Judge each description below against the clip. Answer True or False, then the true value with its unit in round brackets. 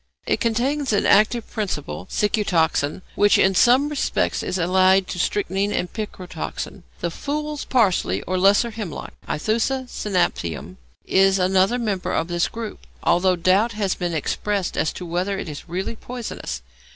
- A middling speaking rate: True (150 wpm)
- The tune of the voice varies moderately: True (3.9 semitones)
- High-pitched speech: True (195 Hz)